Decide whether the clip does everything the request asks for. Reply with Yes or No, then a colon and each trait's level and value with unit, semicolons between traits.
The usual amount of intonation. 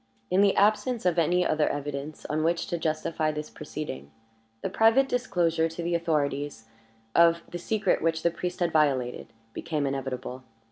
Yes: average, 3.0 semitones